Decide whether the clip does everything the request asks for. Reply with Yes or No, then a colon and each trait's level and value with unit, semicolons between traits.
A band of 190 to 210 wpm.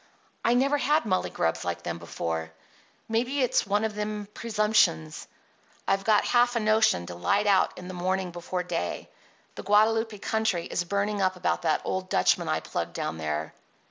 No: average, 175 wpm